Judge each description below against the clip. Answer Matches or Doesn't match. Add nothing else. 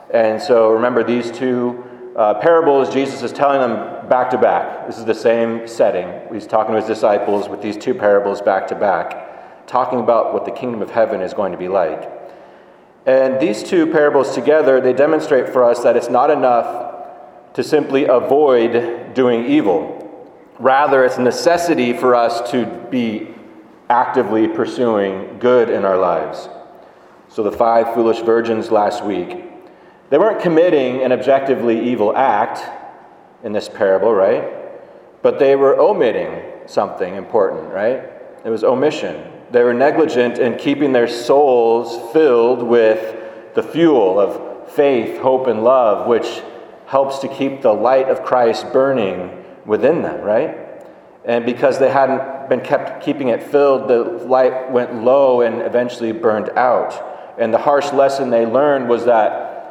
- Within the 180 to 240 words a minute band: Doesn't match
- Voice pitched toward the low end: Matches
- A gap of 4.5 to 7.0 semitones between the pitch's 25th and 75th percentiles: Doesn't match